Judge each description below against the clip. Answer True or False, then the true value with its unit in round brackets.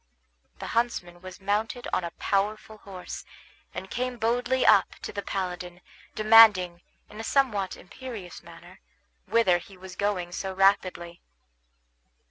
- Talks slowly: True (130 wpm)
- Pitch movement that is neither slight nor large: True (3.8 semitones)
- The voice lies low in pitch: False (195 Hz)